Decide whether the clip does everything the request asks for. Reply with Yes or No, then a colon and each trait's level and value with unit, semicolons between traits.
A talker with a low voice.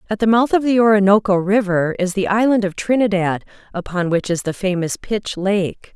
No: high, 200 Hz